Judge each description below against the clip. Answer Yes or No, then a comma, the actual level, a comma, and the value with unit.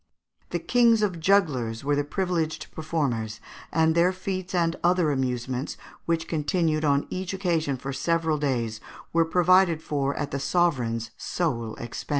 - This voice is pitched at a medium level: Yes, medium, 160 Hz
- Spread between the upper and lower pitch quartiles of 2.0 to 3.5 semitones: No, average, 4.5 semitones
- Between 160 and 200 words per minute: No, average, 150 wpm